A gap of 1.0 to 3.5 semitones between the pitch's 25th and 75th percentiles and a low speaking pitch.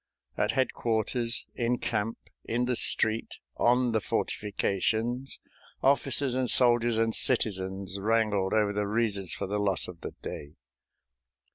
Yes: average, 3.1 semitones; low, 110 Hz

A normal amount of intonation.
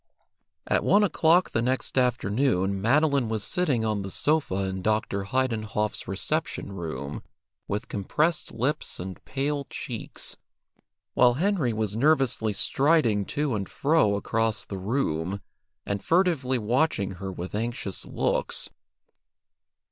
No: wide, 6.1 semitones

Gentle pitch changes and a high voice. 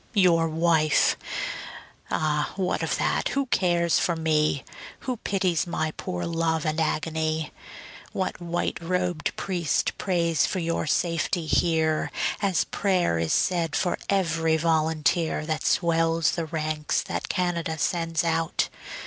No: narrow, 1.8 semitones; medium, 165 Hz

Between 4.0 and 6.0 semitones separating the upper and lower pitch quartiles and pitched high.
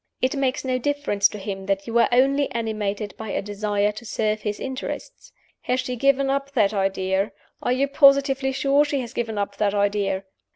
Yes: average, 4.8 semitones; high, 230 Hz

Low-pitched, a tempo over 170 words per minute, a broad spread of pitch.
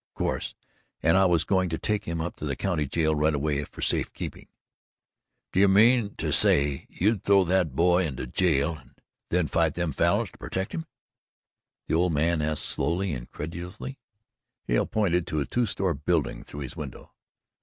No: very low, 85 Hz; average, 185 wpm; average, 4.1 semitones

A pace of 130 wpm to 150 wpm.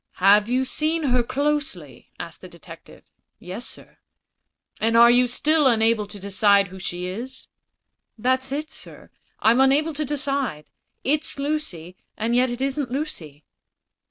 Yes: average, 140 wpm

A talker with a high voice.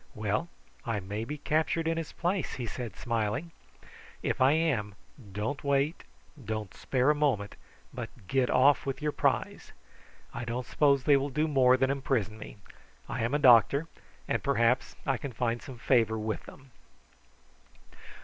No: low, 130 Hz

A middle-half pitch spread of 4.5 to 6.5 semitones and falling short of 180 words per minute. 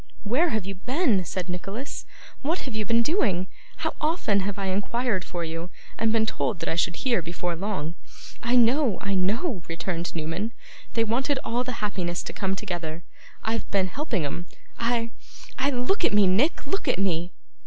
No: average, 5.2 semitones; average, 185 wpm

